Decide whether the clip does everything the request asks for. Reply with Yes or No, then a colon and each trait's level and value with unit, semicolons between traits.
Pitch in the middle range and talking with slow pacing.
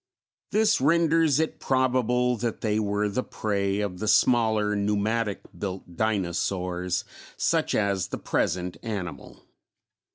No: low, 105 Hz; slow, 120 wpm